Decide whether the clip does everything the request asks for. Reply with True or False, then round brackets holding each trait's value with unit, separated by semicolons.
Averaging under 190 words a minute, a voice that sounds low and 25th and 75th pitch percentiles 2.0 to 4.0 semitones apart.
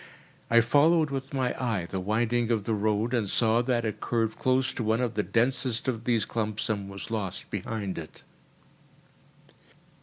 True (175 wpm; 115 Hz; 2.5 semitones)